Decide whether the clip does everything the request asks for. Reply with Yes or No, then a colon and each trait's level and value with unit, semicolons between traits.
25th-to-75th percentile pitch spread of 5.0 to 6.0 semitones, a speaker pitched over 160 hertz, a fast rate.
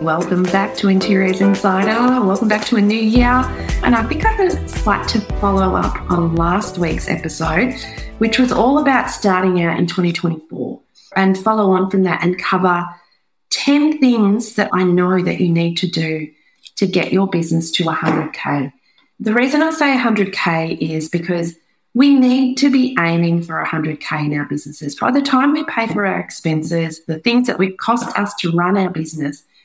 No: average, 5.3 semitones; high, 190 Hz; average, 180 wpm